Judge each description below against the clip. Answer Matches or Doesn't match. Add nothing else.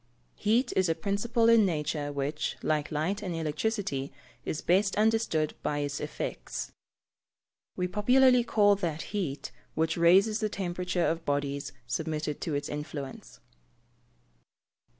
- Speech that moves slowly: Matches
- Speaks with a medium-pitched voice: Matches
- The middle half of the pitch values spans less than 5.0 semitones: Doesn't match